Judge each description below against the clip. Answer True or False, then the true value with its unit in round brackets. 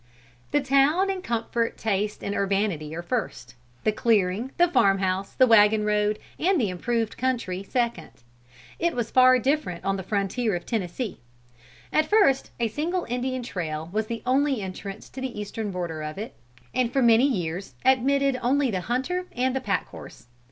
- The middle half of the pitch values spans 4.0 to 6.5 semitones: True (5.0 semitones)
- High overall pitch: True (230 Hz)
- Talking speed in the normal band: True (175 wpm)